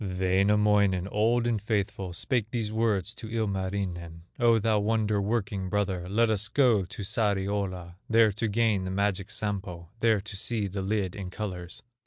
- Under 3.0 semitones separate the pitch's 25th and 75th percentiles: Yes, narrow, 2.6 semitones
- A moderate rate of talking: Yes, average, 160 wpm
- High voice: No, low, 100 Hz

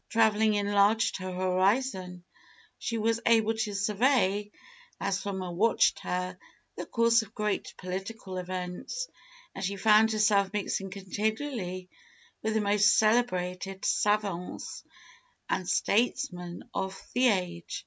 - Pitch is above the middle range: Yes, high, 200 Hz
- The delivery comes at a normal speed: No, slow, 120 wpm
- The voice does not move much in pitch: No, average, 3.0 semitones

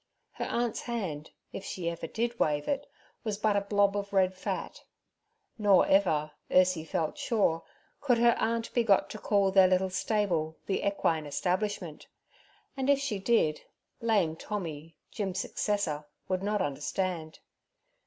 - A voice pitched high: Yes, high, 195 Hz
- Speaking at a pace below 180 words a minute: Yes, average, 145 wpm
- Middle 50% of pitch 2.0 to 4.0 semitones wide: No, average, 4.5 semitones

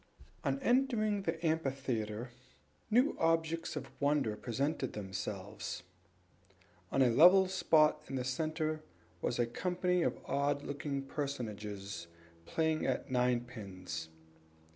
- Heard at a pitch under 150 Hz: Yes, medium, 140 Hz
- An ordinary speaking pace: No, slow, 110 wpm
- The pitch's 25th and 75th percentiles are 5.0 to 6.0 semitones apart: Yes, wide, 5.6 semitones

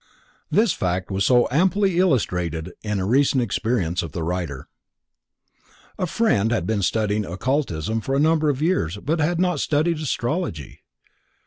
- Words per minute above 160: No, average, 145 wpm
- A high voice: No, low, 120 Hz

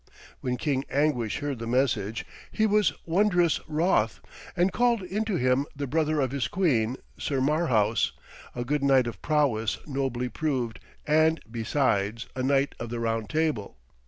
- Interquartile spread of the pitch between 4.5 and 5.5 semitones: Yes, average, 5.1 semitones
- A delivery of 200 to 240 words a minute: No, average, 155 wpm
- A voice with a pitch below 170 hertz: Yes, low, 135 Hz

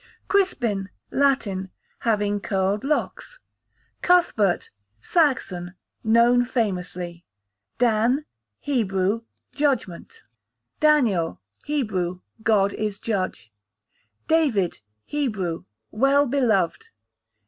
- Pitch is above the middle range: Yes, high, 215 Hz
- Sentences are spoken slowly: Yes, slow, 70 wpm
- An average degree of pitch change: No, wide, 6.3 semitones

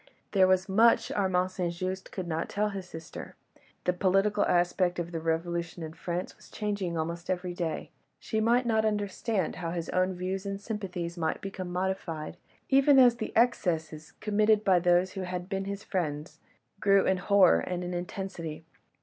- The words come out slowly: No, average, 175 wpm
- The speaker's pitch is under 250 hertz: Yes, medium, 185 Hz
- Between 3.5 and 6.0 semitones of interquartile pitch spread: No, average, 2.7 semitones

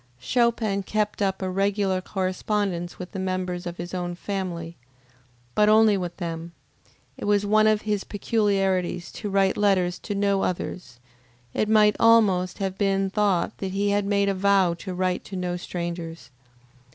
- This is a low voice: No, high, 195 Hz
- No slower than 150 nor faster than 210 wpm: Yes, average, 165 wpm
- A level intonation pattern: Yes, narrow, 2.2 semitones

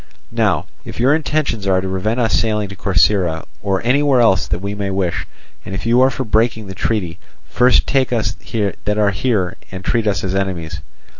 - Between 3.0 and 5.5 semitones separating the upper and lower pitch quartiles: Yes, average, 3.8 semitones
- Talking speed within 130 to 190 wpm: No, average, 200 wpm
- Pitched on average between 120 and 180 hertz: No, low, 105 Hz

